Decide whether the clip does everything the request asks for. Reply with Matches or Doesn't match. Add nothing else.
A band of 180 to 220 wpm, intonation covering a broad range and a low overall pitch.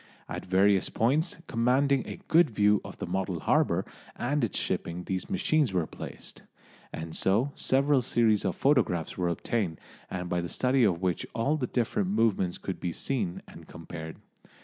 Doesn't match